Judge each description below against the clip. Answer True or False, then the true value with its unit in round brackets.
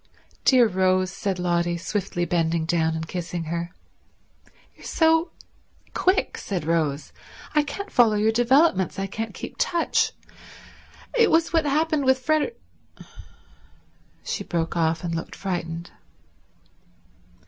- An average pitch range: False (8.4 semitones)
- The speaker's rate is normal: False (125 wpm)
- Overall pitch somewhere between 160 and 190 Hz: True (185 Hz)